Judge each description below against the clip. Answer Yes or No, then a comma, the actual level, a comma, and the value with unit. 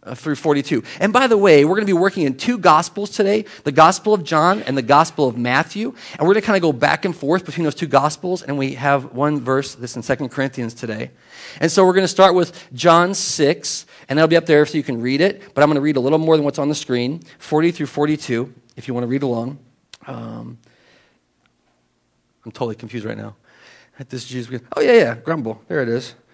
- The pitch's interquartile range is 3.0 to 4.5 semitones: No, average, 5.1 semitones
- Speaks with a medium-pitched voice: Yes, medium, 150 Hz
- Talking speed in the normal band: No, fast, 235 wpm